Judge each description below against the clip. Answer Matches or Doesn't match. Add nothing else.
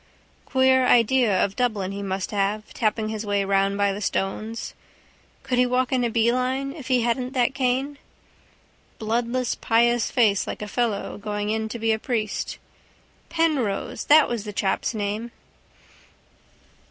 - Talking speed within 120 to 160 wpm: Matches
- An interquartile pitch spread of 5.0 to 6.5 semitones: Doesn't match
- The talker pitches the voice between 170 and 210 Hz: Doesn't match